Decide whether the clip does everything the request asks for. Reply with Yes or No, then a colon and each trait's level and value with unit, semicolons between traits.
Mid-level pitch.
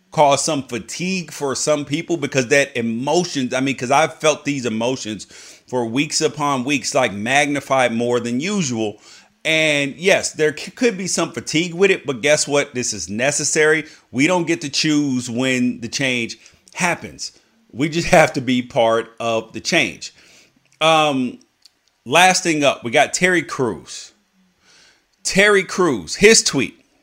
Yes: medium, 145 Hz